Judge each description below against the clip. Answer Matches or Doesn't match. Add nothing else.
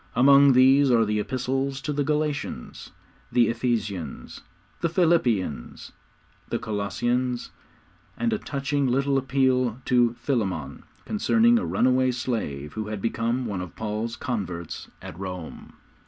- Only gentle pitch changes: Doesn't match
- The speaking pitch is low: Matches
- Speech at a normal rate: Doesn't match